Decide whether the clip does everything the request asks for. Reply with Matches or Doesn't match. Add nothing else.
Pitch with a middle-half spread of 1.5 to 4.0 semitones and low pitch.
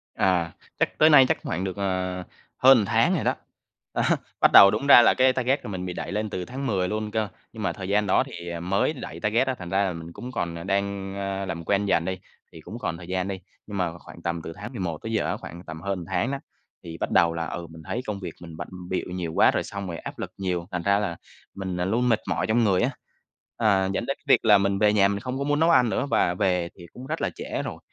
Matches